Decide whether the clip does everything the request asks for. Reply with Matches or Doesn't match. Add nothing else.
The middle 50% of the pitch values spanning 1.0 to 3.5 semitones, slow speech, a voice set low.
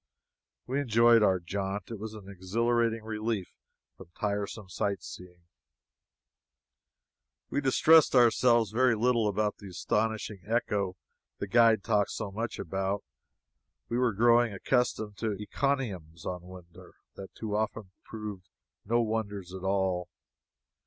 Matches